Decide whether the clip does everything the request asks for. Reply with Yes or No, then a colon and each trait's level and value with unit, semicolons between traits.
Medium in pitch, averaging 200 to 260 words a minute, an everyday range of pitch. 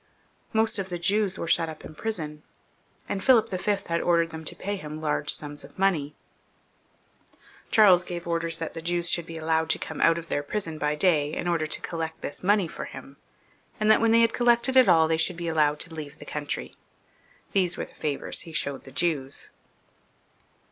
Yes: medium, 165 Hz; fast, 205 wpm; average, 3.6 semitones